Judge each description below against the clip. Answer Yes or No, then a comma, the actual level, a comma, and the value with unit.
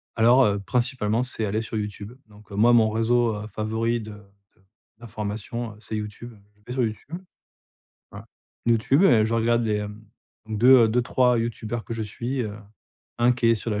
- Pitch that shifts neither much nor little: No, narrow, 2.1 semitones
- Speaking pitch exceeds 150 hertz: No, low, 110 Hz